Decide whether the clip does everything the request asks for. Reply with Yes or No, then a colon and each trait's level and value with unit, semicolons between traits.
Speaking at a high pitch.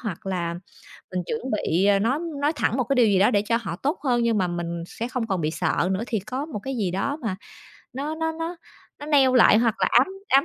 Yes: high, 230 Hz